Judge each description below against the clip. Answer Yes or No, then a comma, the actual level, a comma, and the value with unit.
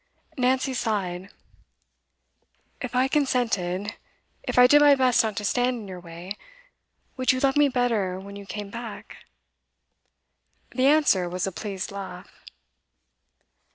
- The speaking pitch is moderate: No, high, 220 Hz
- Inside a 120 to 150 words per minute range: Yes, slow, 135 wpm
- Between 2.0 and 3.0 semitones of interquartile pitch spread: No, average, 5.0 semitones